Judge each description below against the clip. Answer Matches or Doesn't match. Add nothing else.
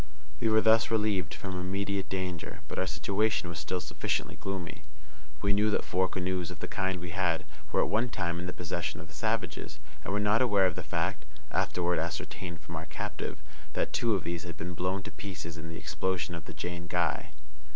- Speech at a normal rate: Doesn't match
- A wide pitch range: Doesn't match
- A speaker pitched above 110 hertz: Doesn't match